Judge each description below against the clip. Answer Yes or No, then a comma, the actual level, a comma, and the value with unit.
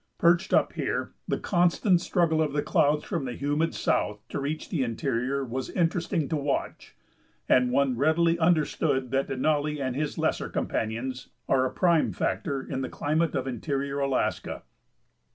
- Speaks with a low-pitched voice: No, medium, 145 Hz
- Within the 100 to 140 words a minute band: No, average, 160 wpm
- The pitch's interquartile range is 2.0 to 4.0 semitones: Yes, average, 3.6 semitones